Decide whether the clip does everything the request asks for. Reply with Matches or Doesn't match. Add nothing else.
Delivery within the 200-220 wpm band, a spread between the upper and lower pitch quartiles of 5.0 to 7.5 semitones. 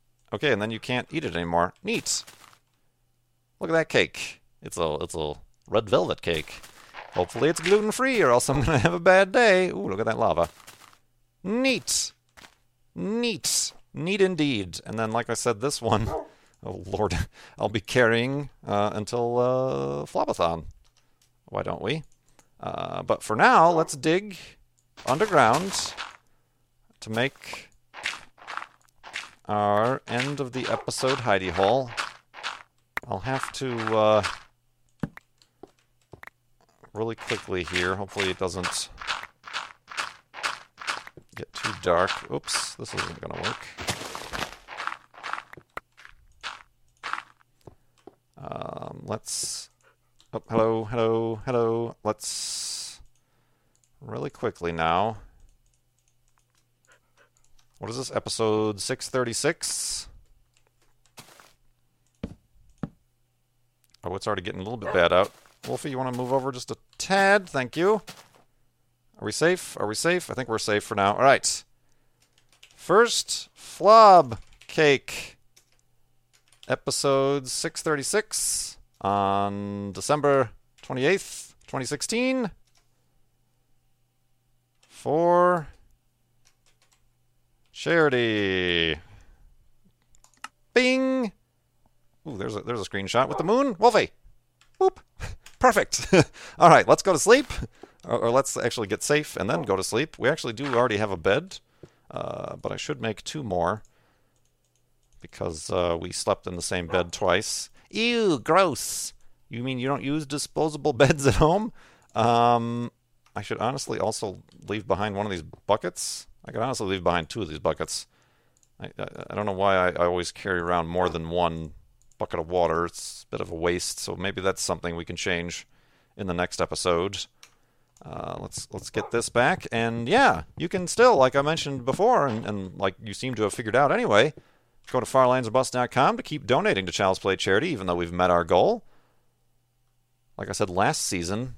Doesn't match